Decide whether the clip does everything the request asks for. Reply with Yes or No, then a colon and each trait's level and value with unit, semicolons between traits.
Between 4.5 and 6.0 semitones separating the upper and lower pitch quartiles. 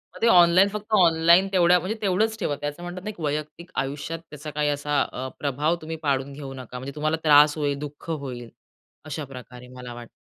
No: average, 3.7 semitones